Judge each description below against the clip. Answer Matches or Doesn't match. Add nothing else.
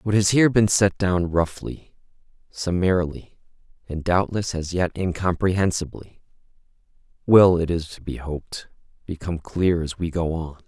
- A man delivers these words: Matches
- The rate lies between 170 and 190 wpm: Doesn't match